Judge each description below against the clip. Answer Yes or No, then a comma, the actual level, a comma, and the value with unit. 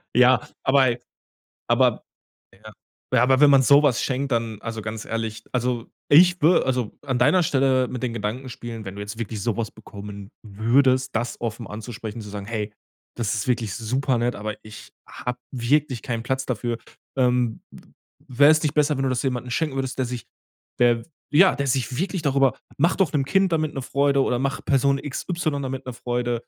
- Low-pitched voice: Yes, low, 125 Hz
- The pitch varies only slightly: No, average, 3.3 semitones